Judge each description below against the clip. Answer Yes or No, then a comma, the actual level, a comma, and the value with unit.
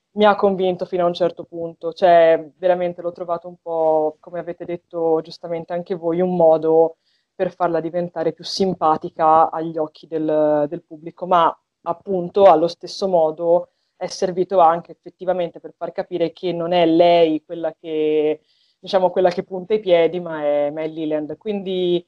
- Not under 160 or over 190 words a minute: Yes, average, 165 wpm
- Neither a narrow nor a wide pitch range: No, narrow, 1.8 semitones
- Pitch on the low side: No, medium, 170 Hz